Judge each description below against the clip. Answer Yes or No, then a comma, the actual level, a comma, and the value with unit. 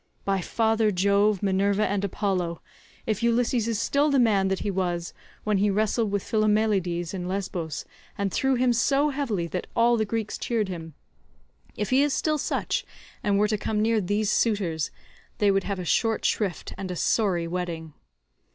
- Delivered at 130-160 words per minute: No, average, 175 wpm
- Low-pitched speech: No, high, 205 Hz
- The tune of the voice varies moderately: Yes, average, 3.5 semitones